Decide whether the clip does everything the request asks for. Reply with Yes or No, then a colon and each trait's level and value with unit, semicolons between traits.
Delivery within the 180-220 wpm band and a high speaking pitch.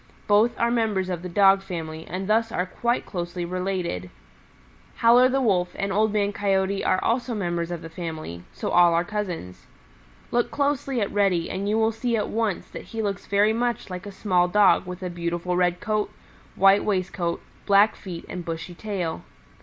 Yes: average, 185 wpm; high, 195 Hz